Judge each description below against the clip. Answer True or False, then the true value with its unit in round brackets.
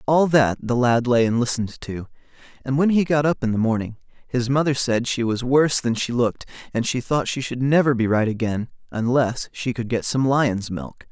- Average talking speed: False (220 wpm)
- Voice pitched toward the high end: False (125 Hz)